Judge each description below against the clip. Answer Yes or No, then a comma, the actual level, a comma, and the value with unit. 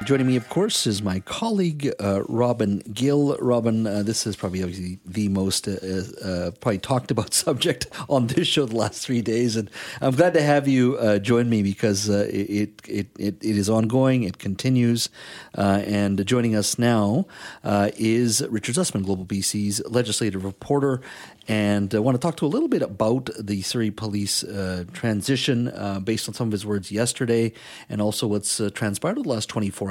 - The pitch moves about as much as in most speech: Yes, average, 3.4 semitones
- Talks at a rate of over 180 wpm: Yes, average, 195 wpm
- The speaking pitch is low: Yes, low, 110 Hz